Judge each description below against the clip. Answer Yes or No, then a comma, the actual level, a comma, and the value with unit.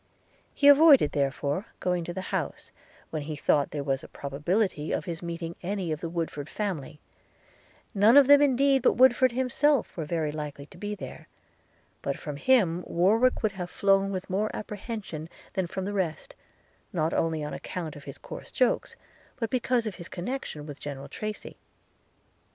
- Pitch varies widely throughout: Yes, wide, 6.6 semitones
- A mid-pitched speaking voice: Yes, medium, 180 Hz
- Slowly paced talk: No, average, 175 wpm